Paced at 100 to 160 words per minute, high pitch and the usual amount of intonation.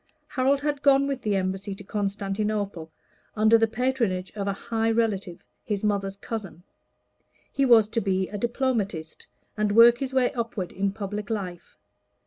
Yes: average, 150 wpm; high, 210 Hz; average, 3.2 semitones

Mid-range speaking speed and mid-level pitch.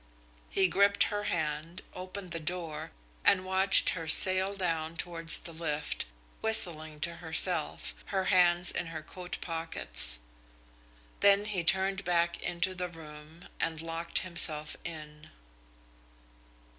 No: slow, 125 wpm; medium, 170 Hz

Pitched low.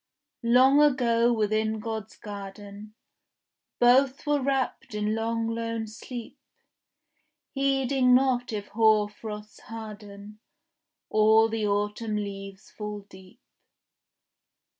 No: high, 220 Hz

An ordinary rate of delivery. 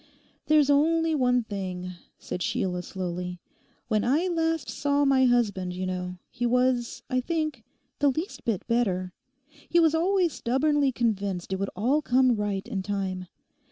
Yes: average, 155 wpm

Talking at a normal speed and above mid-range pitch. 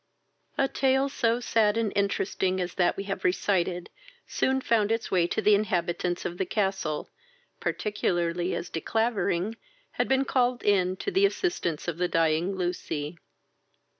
Yes: average, 155 wpm; high, 195 Hz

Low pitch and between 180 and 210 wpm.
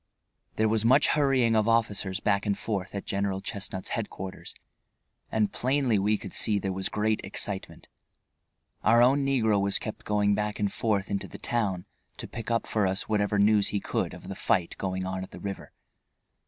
Yes: low, 105 Hz; average, 185 wpm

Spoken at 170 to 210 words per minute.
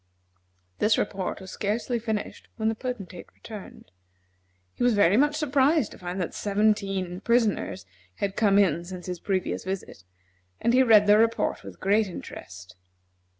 No: average, 150 wpm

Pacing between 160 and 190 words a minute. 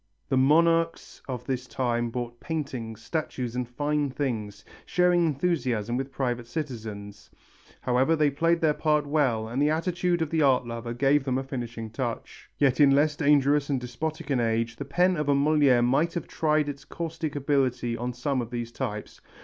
Yes: average, 180 wpm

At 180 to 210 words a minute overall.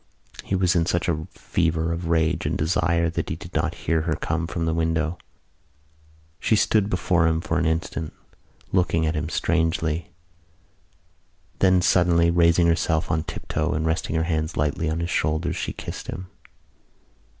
No: average, 165 wpm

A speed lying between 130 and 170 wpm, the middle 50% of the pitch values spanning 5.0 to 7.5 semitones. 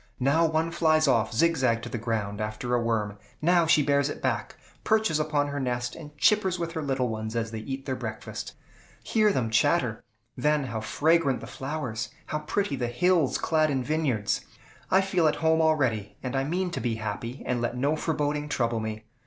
No: average, 195 wpm; average, 5.3 semitones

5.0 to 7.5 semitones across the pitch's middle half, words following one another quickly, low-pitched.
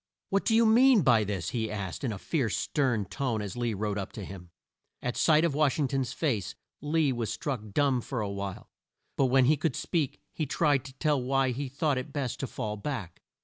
Yes: average, 5.3 semitones; fast, 230 wpm; low, 130 Hz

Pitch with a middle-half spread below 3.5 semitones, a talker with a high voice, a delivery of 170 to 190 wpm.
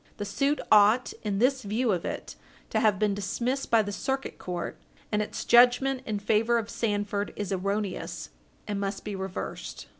Yes: average, 3.0 semitones; high, 210 Hz; average, 175 wpm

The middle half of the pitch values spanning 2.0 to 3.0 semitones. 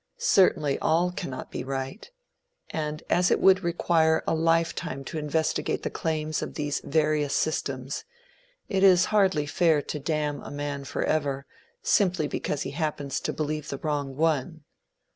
Yes: narrow, 2.5 semitones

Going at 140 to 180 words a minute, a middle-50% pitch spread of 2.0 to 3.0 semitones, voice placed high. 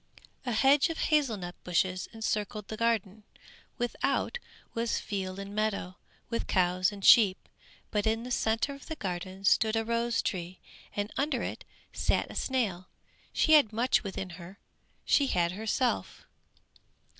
No: average, 150 wpm; average, 4.0 semitones; high, 215 Hz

